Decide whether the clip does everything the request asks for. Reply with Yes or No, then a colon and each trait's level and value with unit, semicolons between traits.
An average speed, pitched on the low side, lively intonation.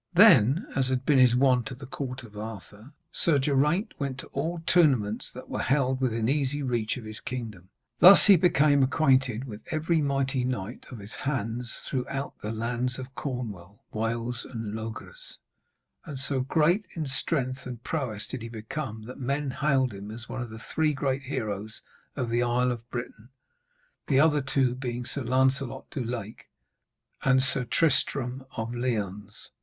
No: average, 170 wpm; low, 130 Hz; average, 3.2 semitones